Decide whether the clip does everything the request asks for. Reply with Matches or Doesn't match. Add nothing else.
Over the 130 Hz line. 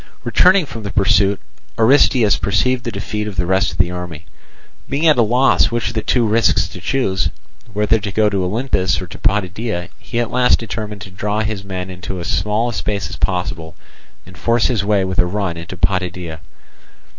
Doesn't match